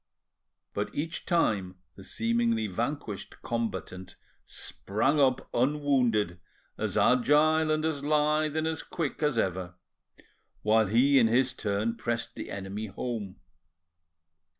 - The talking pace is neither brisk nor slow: No, slow, 120 wpm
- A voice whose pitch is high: No, low, 120 Hz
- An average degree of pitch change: No, wide, 6.0 semitones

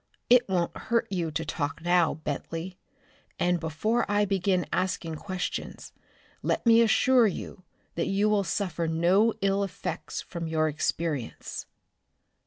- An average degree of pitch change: Yes, average, 3.8 semitones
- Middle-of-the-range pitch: Yes, medium, 180 Hz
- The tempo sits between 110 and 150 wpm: Yes, slow, 135 wpm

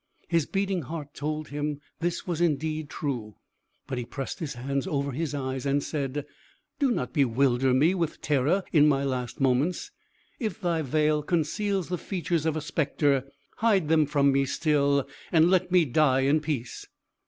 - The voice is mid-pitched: Yes, medium, 150 Hz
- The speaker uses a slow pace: No, average, 170 wpm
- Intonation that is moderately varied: Yes, average, 3.3 semitones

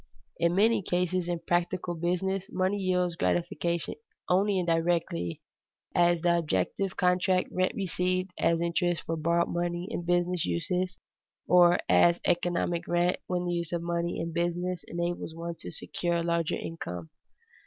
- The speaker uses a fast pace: No, average, 145 wpm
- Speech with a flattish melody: Yes, narrow, 1.1 semitones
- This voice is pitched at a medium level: Yes, medium, 175 Hz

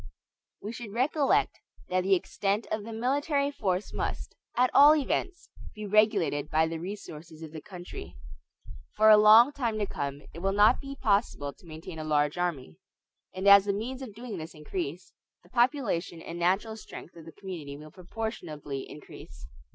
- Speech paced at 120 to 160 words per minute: No, average, 175 wpm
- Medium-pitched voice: No, high, 195 Hz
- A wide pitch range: Yes, wide, 5.8 semitones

